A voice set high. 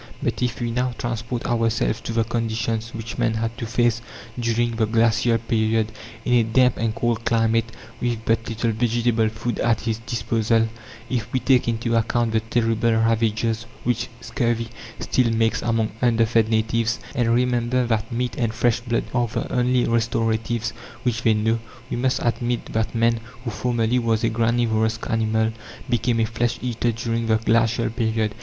No: low, 115 Hz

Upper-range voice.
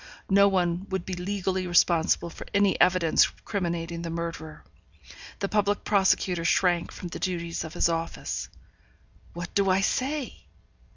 No: medium, 180 Hz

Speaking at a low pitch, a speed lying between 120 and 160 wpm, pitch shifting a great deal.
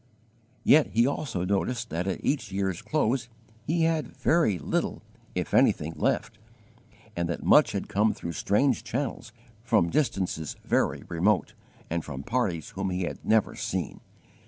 Yes: low, 100 Hz; average, 150 wpm; wide, 6.6 semitones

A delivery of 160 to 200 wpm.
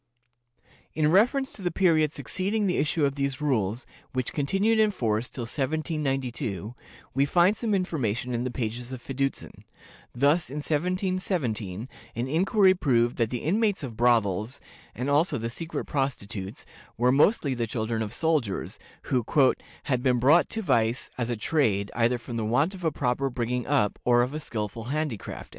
Yes: average, 165 wpm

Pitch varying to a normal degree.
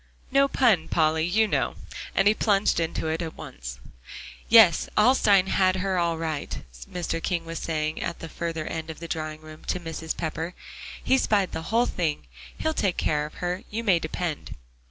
Yes: average, 3.6 semitones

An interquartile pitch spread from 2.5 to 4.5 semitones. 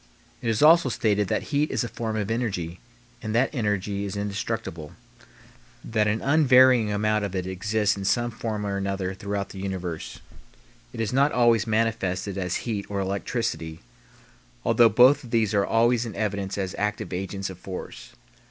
Yes: average, 2.9 semitones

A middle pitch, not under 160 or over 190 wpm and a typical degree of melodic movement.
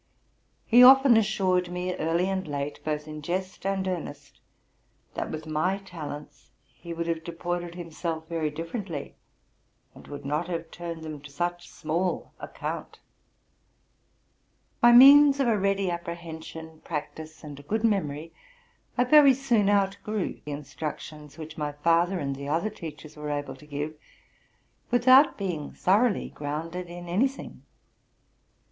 No: medium, 170 Hz; average, 145 wpm; average, 4.2 semitones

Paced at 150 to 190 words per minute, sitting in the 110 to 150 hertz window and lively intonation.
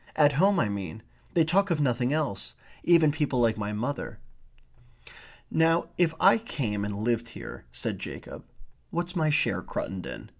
Yes: average, 160 wpm; medium, 140 Hz; wide, 7.2 semitones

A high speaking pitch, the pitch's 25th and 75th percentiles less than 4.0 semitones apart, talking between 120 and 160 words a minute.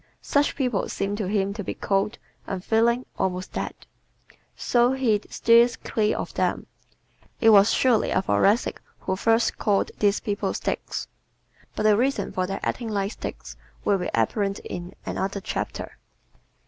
Yes: high, 205 Hz; average, 3.0 semitones; average, 150 wpm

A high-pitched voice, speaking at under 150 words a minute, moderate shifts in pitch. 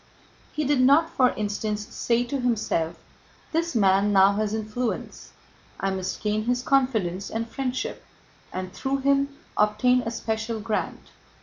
Yes: high, 225 Hz; average, 140 wpm; average, 3.5 semitones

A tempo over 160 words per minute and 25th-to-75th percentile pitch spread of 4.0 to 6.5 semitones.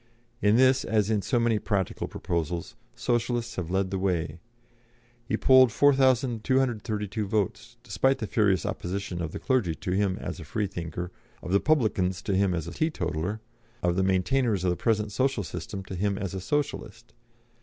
Yes: average, 170 wpm; average, 4.5 semitones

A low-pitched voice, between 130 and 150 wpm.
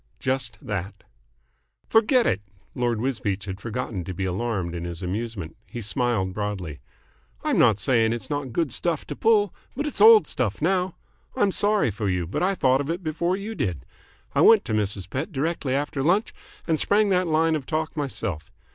No: low, 125 Hz; average, 185 wpm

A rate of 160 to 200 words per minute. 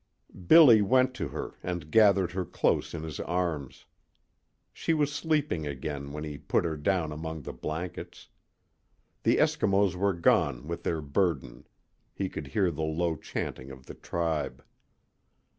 No: average, 150 wpm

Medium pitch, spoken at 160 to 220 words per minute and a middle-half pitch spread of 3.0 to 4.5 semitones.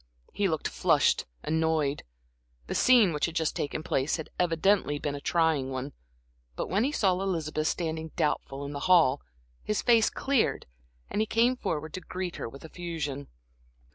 Yes: medium, 160 Hz; average, 170 wpm; average, 4.2 semitones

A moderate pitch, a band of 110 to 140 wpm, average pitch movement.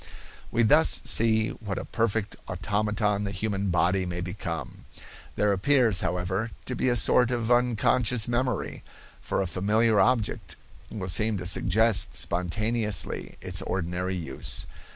No: low, 105 Hz; slow, 135 wpm; average, 3.9 semitones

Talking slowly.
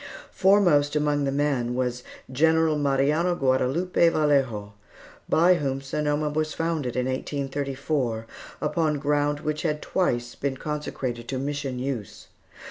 Yes: slow, 125 wpm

